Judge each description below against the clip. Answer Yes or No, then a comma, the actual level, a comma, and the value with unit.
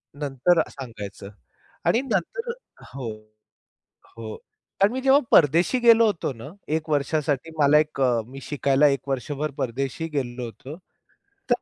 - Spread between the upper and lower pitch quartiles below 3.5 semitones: No, average, 4.4 semitones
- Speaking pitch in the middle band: Yes, medium, 145 Hz